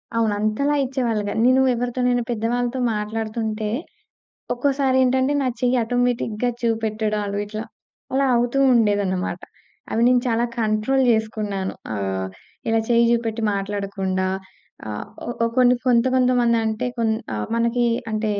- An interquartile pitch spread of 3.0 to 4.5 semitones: No, narrow, 2.6 semitones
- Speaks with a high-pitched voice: Yes, high, 225 Hz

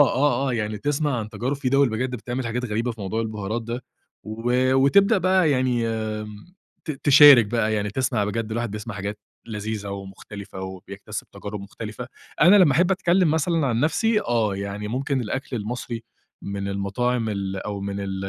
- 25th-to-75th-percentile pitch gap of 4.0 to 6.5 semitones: Yes, average, 4.3 semitones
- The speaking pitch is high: No, low, 115 Hz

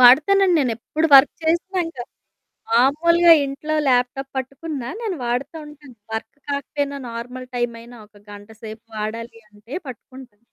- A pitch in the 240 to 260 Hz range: Yes, very high, 255 Hz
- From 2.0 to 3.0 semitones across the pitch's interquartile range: No, average, 4.3 semitones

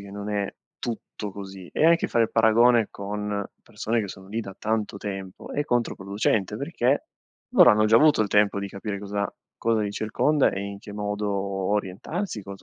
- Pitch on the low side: Yes, low, 105 Hz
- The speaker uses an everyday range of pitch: No, narrow, 2.1 semitones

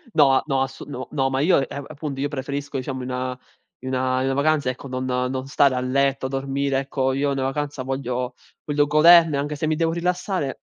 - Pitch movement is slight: Yes, narrow, 1.9 semitones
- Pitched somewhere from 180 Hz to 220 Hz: No, low, 135 Hz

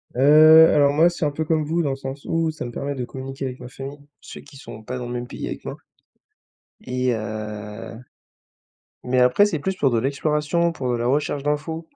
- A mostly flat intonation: No, average, 3.7 semitones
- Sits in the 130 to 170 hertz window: Yes, medium, 140 Hz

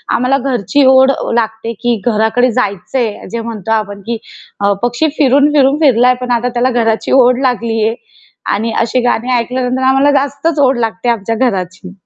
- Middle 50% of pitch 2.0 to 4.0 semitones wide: Yes, average, 2.8 semitones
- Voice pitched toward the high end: Yes, high, 240 Hz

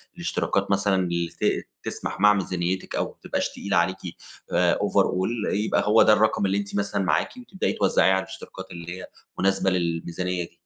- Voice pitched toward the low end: Yes, very low, 95 Hz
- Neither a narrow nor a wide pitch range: No, narrow, 2.1 semitones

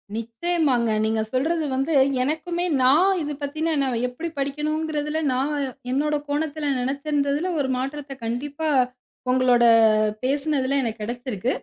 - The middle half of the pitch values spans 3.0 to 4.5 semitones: Yes, average, 3.3 semitones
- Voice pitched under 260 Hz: No, very high, 280 Hz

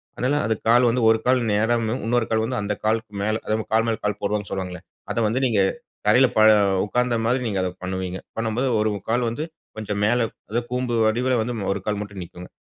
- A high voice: No, low, 110 Hz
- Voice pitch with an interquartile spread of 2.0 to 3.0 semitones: Yes, average, 2.7 semitones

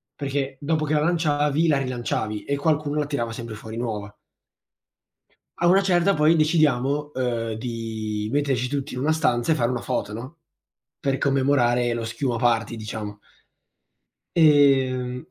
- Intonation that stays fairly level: No, average, 4.1 semitones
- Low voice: Yes, low, 130 Hz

